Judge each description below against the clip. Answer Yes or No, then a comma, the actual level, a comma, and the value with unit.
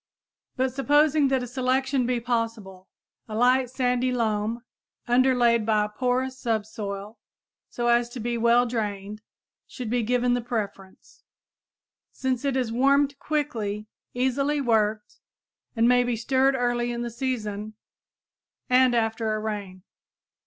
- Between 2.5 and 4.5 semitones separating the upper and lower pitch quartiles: Yes, average, 2.9 semitones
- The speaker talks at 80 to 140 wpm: Yes, slow, 135 wpm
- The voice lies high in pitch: Yes, high, 240 Hz